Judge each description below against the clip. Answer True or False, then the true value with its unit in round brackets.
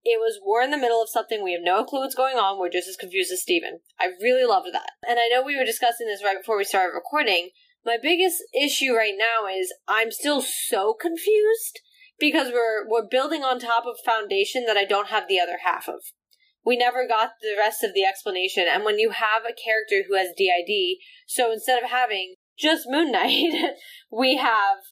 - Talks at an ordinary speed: False (215 wpm)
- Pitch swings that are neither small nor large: False (8.7 semitones)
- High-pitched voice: True (245 Hz)